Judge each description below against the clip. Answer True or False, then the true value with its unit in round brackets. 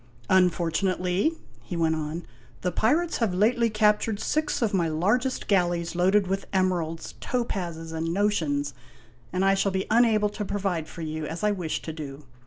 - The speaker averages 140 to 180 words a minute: True (175 wpm)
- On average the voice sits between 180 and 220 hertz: True (185 Hz)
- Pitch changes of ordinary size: True (4.3 semitones)